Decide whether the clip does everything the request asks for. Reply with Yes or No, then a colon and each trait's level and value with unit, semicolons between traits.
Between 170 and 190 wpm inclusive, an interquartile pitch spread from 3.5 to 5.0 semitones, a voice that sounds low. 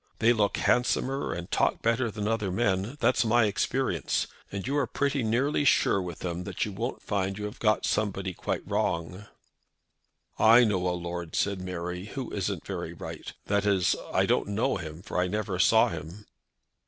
Yes: average, 180 wpm; average, 4.2 semitones; low, 100 Hz